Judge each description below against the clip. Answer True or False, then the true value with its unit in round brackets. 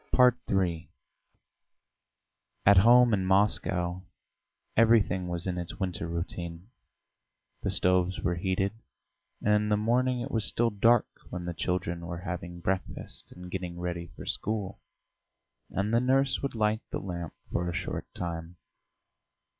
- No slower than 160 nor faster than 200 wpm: False (140 wpm)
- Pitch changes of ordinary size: True (3.6 semitones)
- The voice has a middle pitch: False (95 Hz)